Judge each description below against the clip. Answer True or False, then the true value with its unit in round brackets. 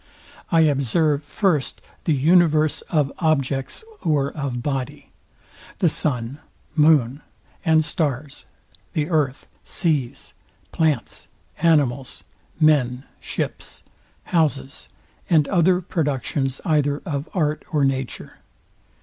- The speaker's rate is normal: False (100 wpm)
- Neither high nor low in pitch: True (150 Hz)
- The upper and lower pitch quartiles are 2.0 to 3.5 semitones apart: True (2.7 semitones)